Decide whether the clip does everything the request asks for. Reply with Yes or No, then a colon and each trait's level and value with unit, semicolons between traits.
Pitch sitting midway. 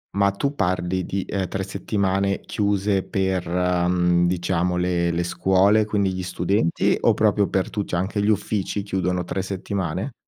No: very low, 95 Hz